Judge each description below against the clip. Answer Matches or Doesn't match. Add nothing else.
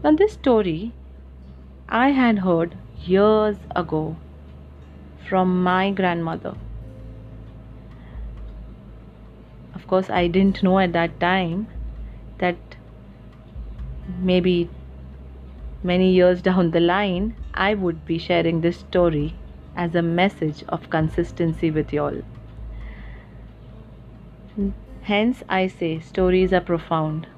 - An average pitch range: Doesn't match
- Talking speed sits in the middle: Doesn't match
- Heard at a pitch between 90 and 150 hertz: Doesn't match